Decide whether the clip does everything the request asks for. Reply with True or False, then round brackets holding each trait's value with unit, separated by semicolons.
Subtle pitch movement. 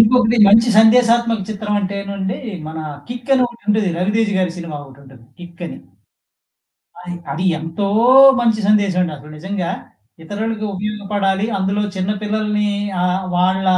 False (3.2 semitones)